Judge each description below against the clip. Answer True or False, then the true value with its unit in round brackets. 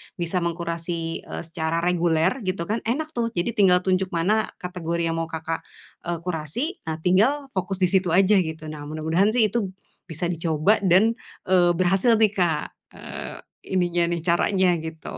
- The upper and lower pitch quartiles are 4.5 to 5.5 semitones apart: False (2.9 semitones)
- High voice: False (180 Hz)